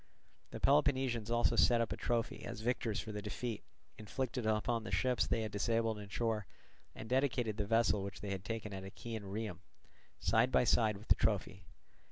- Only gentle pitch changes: Yes, narrow, 2.2 semitones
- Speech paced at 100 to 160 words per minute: No, average, 190 wpm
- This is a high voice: No, low, 110 Hz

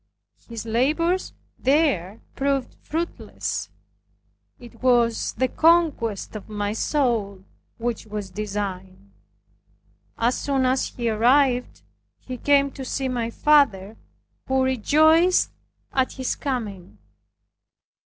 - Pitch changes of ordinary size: Yes, average, 4.6 semitones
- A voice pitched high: Yes, very high, 250 Hz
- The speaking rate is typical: No, slow, 100 wpm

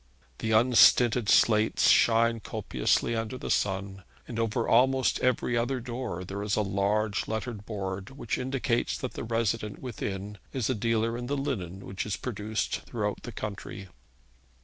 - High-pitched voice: No, low, 110 Hz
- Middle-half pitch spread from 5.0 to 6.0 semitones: No, average, 3.2 semitones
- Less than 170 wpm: Yes, average, 155 wpm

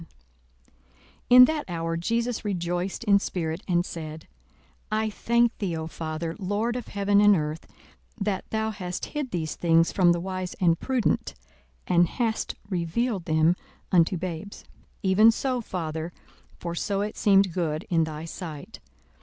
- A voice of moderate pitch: Yes, medium, 180 Hz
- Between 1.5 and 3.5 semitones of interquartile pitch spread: No, average, 4.3 semitones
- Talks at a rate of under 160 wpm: Yes, average, 150 wpm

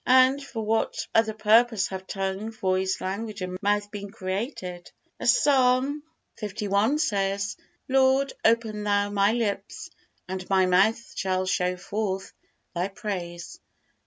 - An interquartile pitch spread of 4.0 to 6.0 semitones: No, average, 3.2 semitones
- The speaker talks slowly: Yes, slow, 130 wpm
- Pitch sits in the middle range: No, high, 205 Hz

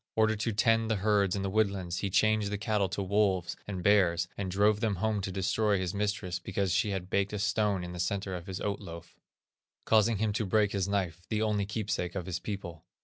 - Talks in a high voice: No, low, 100 Hz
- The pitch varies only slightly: Yes, narrow, 2.3 semitones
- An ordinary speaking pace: No, fast, 225 wpm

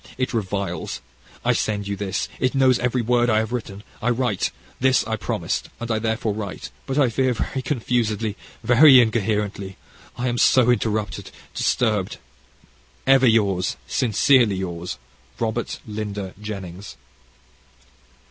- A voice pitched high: No, low, 110 Hz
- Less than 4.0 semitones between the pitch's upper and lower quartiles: Yes, average, 3.3 semitones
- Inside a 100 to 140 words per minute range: Yes, slow, 135 wpm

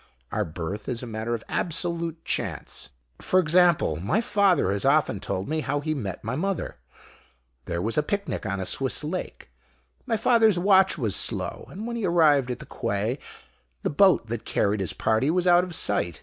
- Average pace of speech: Yes, average, 190 wpm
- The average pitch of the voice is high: No, medium, 150 Hz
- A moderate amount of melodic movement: No, wide, 8.7 semitones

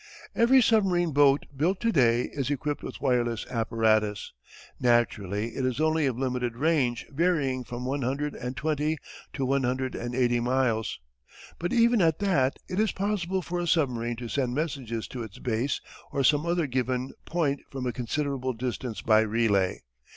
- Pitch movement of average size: Yes, average, 4.6 semitones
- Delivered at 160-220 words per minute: Yes, average, 170 wpm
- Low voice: Yes, low, 130 Hz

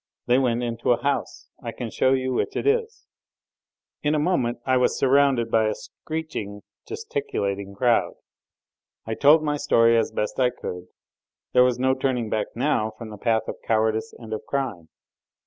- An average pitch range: Yes, average, 4.1 semitones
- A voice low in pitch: Yes, low, 125 Hz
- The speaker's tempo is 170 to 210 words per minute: Yes, average, 180 wpm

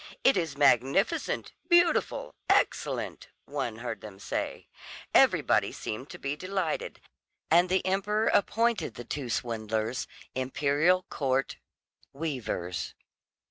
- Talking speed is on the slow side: Yes, slow, 105 wpm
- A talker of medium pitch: Yes, medium, 145 Hz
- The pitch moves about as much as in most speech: No, wide, 7.4 semitones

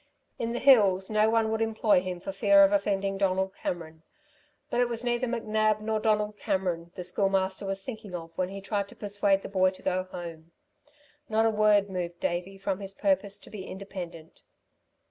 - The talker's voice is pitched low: No, high, 195 Hz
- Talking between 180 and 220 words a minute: Yes, average, 190 wpm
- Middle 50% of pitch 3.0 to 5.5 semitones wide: No, narrow, 2.5 semitones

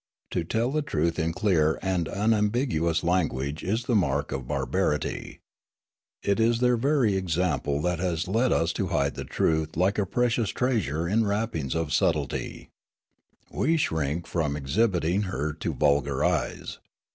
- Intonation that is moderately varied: No, wide, 6.1 semitones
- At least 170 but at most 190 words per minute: No, average, 155 wpm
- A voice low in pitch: Yes, very low, 90 Hz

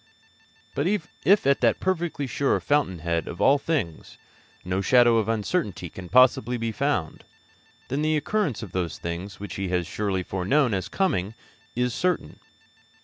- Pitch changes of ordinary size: No, wide, 7.5 semitones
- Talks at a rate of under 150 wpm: No, average, 155 wpm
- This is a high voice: No, low, 115 Hz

